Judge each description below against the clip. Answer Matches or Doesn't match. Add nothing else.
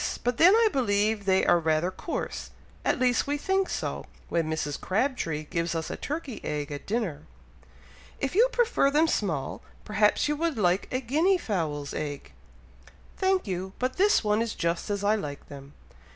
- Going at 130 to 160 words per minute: Doesn't match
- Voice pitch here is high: Matches